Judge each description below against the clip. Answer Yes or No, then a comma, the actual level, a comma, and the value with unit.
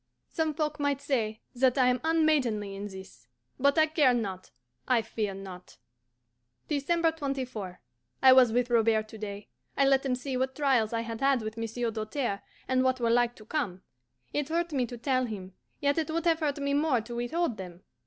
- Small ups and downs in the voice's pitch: No, average, 4.6 semitones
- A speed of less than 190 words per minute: No, average, 195 wpm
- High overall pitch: Yes, very high, 250 Hz